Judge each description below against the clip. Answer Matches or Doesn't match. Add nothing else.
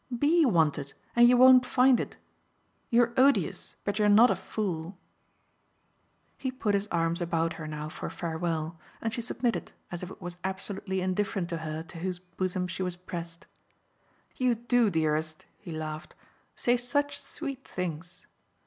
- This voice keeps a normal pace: Matches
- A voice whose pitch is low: Doesn't match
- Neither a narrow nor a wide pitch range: Doesn't match